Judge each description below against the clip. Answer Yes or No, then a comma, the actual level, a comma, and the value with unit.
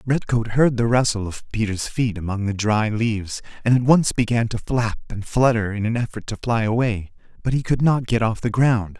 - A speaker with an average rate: No, fast, 220 wpm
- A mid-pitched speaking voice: No, low, 115 Hz